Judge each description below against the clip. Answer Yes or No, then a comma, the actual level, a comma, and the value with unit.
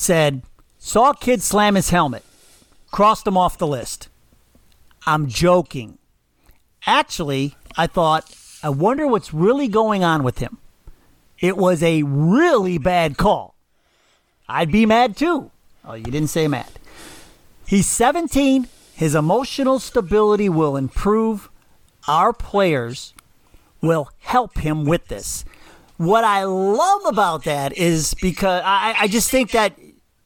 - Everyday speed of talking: No, slow, 130 wpm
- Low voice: No, medium, 180 Hz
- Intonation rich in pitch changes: Yes, wide, 6.0 semitones